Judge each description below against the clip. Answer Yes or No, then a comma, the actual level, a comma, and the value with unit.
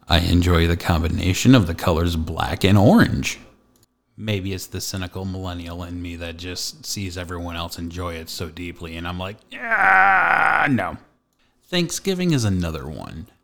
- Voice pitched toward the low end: Yes, very low, 90 Hz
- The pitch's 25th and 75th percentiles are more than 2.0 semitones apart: Yes, average, 2.8 semitones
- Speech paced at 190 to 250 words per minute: No, average, 155 wpm